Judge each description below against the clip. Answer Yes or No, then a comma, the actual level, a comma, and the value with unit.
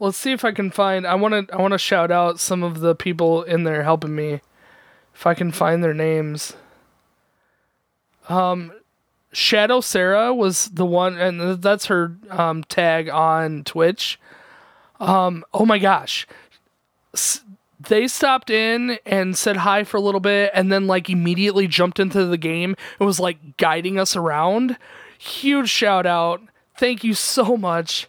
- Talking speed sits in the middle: Yes, average, 165 wpm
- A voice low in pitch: No, medium, 185 Hz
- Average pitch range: Yes, average, 3.4 semitones